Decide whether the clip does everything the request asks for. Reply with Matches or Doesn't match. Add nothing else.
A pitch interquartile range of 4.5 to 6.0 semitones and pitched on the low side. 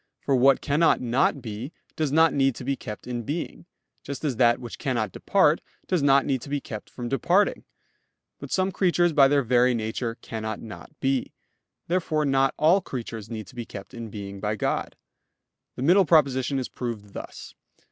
Doesn't match